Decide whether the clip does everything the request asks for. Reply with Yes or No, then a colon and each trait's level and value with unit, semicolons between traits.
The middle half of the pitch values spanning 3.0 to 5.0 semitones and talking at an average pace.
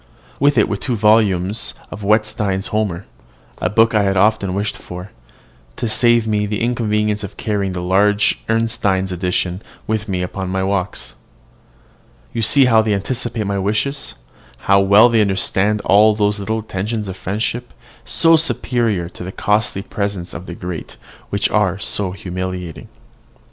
No: narrow, 2.5 semitones; average, 160 wpm